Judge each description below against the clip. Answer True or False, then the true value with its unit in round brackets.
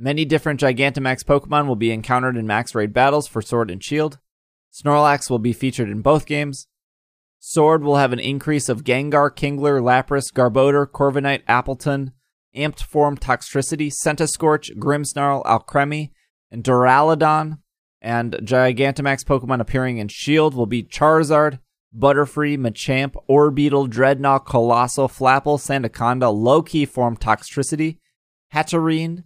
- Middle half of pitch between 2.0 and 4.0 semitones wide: True (2.8 semitones)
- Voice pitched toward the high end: False (140 Hz)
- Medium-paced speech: False (130 wpm)